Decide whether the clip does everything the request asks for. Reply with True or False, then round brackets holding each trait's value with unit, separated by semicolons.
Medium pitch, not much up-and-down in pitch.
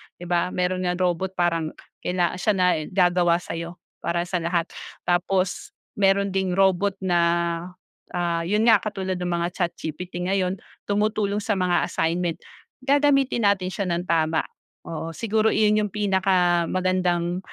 True (180 Hz; 2.2 semitones)